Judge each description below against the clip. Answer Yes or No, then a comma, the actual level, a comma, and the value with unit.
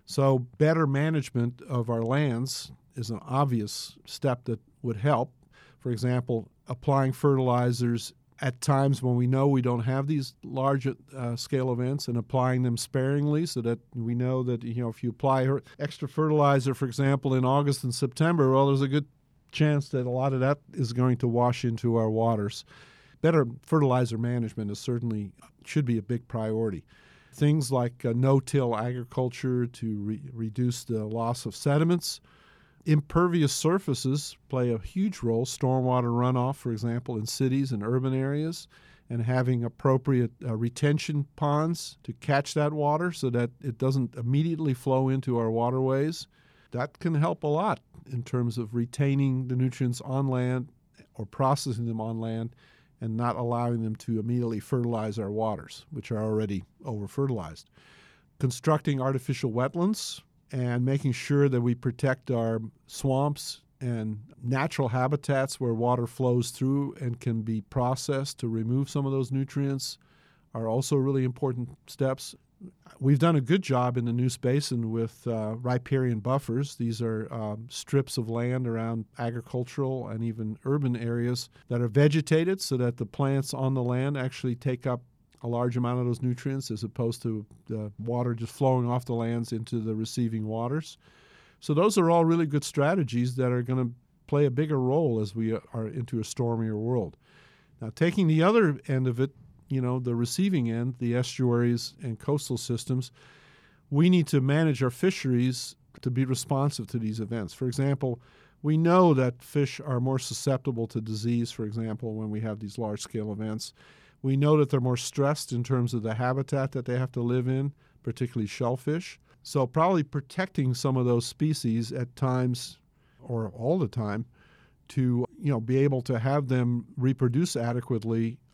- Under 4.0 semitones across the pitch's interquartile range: Yes, average, 2.9 semitones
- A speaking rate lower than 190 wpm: Yes, average, 170 wpm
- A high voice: No, low, 130 Hz